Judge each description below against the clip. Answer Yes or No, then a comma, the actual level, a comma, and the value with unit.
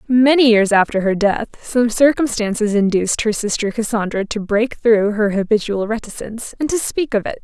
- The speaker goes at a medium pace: Yes, average, 180 wpm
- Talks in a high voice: Yes, high, 220 Hz